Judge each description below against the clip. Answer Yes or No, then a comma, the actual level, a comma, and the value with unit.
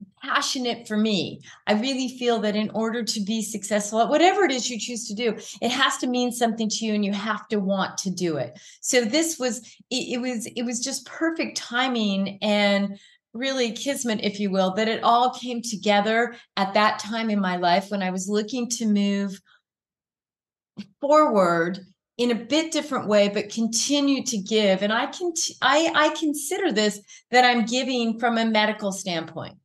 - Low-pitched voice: No, high, 225 Hz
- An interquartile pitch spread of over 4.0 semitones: No, average, 3.5 semitones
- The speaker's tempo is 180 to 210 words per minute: Yes, average, 190 wpm